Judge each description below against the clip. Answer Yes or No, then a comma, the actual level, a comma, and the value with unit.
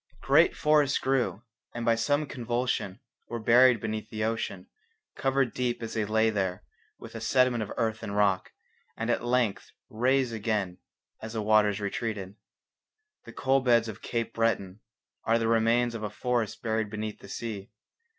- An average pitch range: No, narrow, 2.1 semitones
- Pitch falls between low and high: No, low, 115 Hz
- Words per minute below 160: No, average, 165 wpm